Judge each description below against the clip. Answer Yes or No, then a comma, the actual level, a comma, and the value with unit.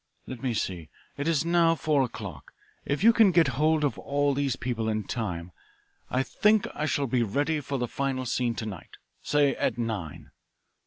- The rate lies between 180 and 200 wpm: Yes, average, 190 wpm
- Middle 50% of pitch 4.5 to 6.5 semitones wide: Yes, average, 4.8 semitones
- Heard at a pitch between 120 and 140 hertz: Yes, low, 135 Hz